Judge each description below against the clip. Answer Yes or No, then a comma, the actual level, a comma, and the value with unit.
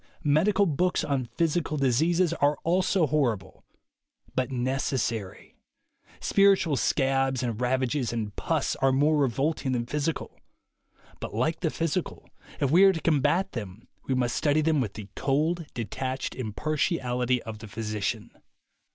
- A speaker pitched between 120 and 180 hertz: Yes, low, 135 Hz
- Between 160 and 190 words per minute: No, average, 145 wpm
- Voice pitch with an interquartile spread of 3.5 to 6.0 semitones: Yes, average, 4.5 semitones